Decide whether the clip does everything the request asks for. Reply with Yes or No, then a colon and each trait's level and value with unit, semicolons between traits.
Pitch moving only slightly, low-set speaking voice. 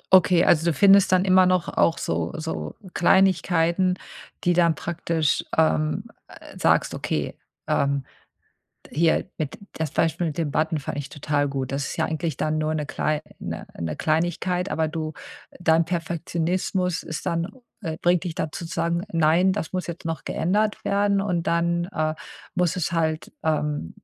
No: narrow, 2.3 semitones; medium, 165 Hz